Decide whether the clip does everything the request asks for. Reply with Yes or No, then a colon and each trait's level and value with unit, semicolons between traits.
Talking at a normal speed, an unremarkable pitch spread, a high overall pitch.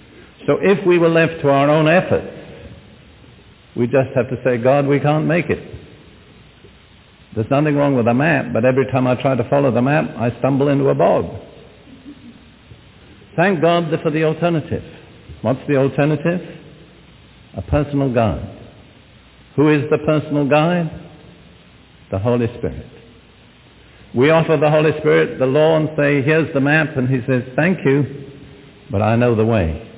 No: average, 160 wpm; average, 4.0 semitones; medium, 140 Hz